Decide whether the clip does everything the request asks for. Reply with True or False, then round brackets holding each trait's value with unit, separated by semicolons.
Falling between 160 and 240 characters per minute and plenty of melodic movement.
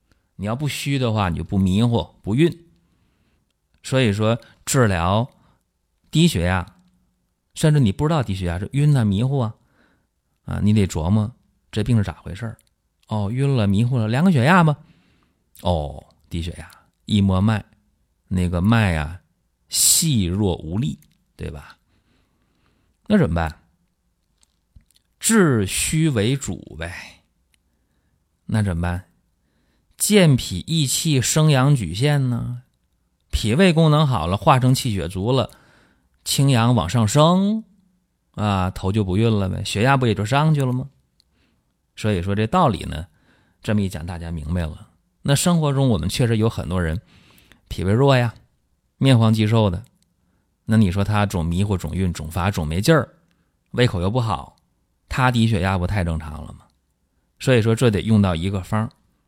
True (210 characters per minute; 6.4 semitones)